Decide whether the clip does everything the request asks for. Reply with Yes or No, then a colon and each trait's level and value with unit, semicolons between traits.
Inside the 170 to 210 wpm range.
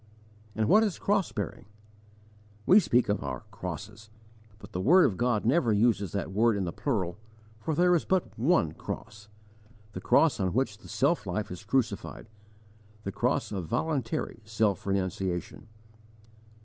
No: average, 155 wpm